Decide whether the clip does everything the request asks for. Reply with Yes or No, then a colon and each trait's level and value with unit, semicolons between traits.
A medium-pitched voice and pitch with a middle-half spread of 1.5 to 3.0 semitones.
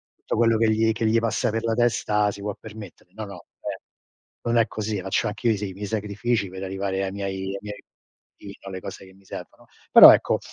No: low, 105 Hz; narrow, 2.5 semitones